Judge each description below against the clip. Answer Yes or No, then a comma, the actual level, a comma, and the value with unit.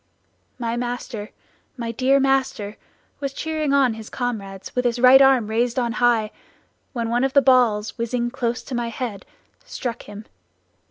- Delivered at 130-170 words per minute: Yes, average, 160 wpm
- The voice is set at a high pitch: Yes, high, 240 Hz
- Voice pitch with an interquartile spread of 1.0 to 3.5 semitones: Yes, narrow, 2.5 semitones